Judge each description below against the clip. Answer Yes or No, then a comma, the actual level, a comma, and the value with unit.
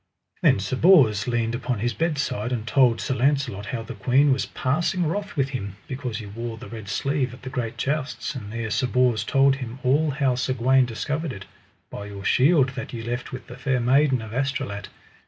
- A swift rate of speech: Yes, fast, 210 wpm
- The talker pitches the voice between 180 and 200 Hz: No, low, 125 Hz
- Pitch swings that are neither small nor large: Yes, average, 3.2 semitones